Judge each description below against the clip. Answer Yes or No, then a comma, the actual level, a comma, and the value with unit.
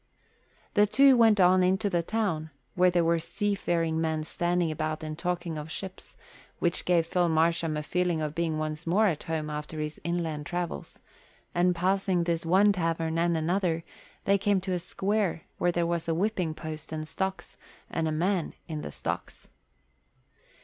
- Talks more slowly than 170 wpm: No, average, 175 wpm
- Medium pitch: Yes, medium, 170 Hz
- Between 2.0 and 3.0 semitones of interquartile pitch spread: Yes, narrow, 2.5 semitones